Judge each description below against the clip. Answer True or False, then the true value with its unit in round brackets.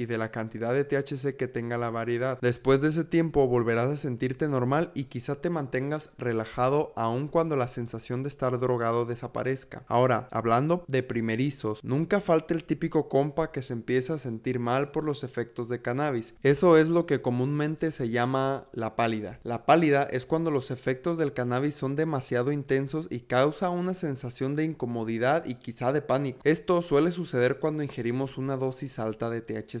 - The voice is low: True (130 Hz)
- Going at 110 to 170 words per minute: False (185 wpm)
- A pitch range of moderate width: True (3.7 semitones)